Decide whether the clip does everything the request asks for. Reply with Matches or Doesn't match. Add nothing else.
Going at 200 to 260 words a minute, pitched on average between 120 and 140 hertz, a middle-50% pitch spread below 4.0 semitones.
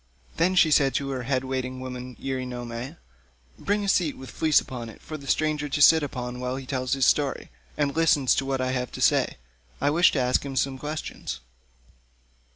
Matches